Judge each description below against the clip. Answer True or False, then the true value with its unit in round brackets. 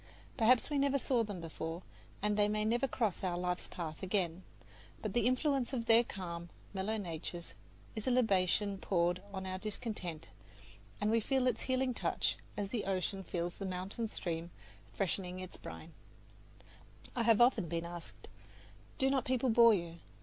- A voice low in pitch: False (205 Hz)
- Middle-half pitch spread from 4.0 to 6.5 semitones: True (4.7 semitones)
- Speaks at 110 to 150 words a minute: False (165 wpm)